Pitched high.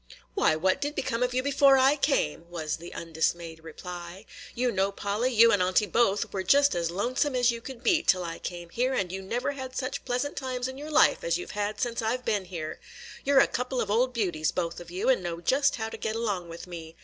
Yes: high, 220 Hz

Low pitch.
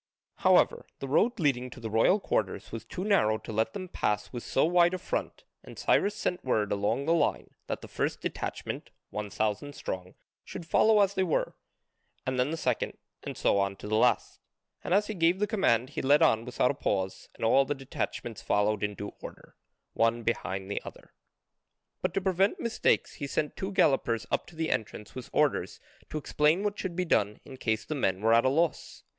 Yes: low, 130 Hz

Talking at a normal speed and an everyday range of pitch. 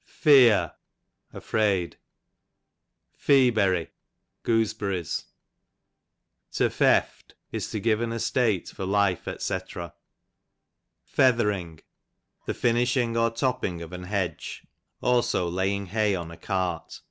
No: slow, 100 wpm; average, 4.2 semitones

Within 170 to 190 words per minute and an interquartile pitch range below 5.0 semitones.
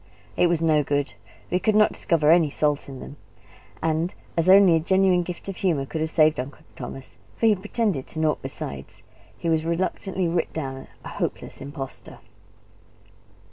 Yes: average, 175 wpm; average, 3.7 semitones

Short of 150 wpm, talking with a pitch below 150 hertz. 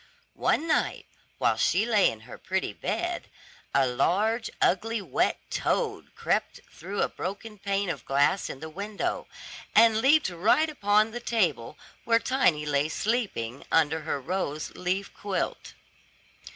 No: average, 140 wpm; high, 195 Hz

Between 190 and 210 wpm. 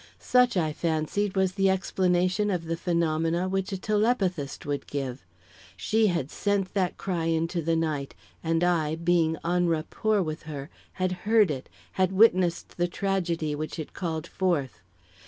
No: average, 155 wpm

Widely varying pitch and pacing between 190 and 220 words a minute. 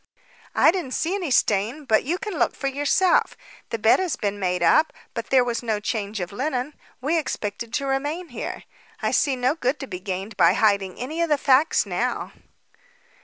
Yes: wide, 6.3 semitones; average, 195 wpm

